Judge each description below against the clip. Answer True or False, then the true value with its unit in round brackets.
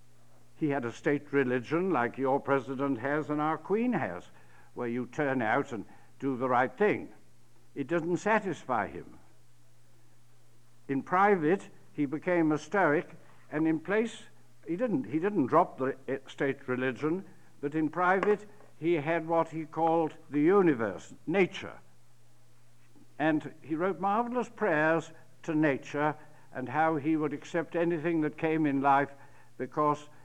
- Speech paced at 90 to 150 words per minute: True (145 wpm)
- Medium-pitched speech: True (150 Hz)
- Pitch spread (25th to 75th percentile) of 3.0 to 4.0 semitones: False (4.5 semitones)